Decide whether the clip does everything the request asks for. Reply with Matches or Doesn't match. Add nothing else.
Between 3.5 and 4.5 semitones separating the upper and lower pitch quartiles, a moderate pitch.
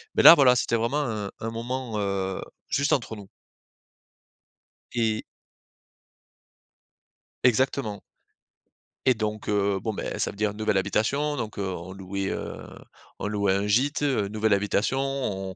Doesn't match